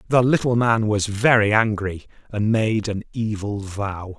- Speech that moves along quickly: No, average, 160 wpm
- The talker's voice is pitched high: No, low, 110 Hz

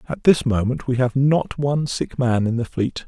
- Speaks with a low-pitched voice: Yes, low, 130 Hz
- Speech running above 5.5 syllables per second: No, 4.8 syllables/s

